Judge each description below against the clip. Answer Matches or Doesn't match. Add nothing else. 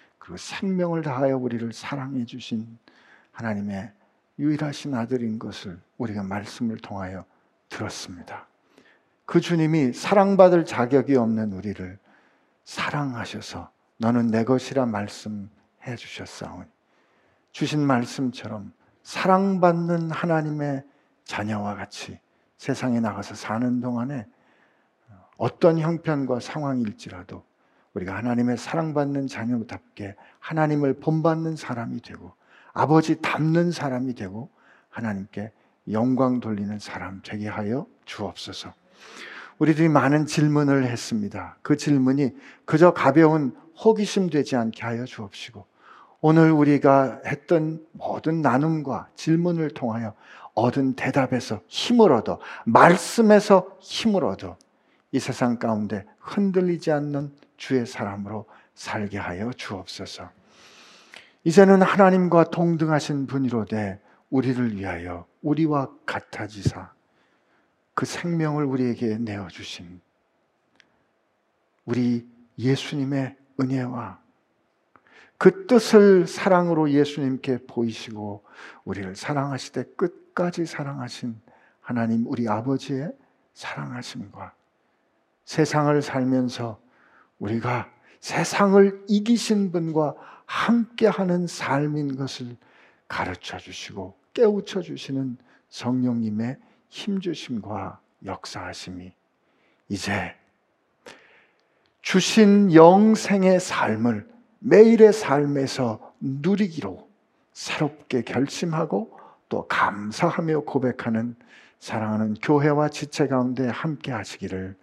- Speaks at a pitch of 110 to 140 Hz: Matches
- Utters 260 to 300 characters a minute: Doesn't match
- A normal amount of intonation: Doesn't match